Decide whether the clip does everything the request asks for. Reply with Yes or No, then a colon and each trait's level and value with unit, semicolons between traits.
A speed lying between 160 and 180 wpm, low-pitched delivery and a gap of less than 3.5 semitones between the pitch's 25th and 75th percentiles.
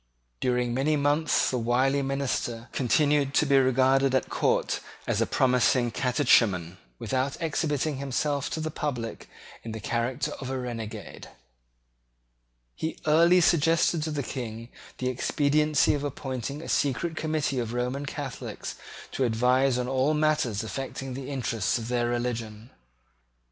No: average, 140 wpm; low, 130 Hz; average, 3.1 semitones